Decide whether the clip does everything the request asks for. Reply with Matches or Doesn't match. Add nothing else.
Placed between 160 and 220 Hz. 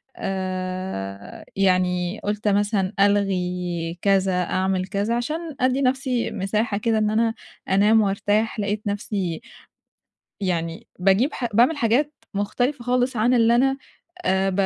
Matches